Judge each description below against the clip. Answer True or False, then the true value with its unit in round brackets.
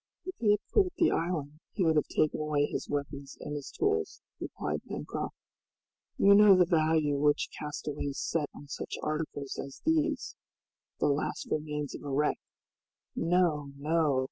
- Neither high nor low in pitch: True (155 Hz)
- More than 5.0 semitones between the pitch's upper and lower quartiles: False (3.8 semitones)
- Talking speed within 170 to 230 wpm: False (160 wpm)